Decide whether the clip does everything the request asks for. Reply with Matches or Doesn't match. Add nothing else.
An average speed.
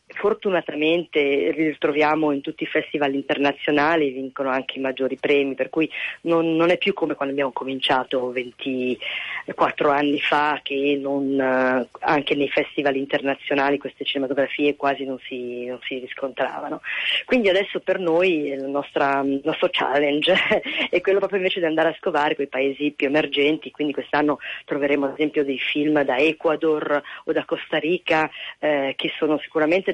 Matches